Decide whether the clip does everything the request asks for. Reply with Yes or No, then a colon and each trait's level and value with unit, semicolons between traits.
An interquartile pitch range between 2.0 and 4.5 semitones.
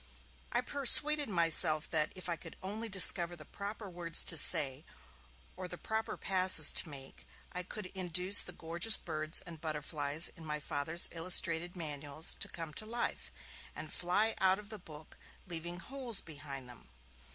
Yes: average, 3.7 semitones